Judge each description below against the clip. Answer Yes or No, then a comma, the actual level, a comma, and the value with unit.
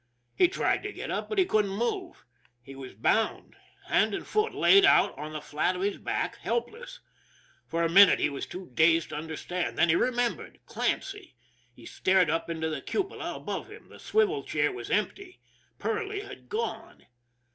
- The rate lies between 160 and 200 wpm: Yes, average, 185 wpm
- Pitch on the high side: Yes, high, 210 Hz